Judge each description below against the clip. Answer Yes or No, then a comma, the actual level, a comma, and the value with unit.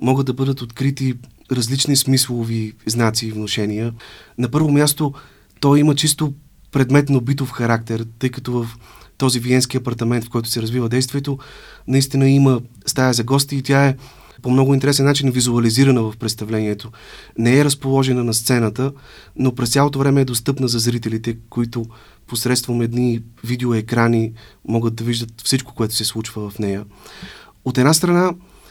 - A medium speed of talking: Yes, average, 155 wpm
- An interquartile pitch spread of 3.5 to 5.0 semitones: No, average, 2.9 semitones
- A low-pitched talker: Yes, low, 125 Hz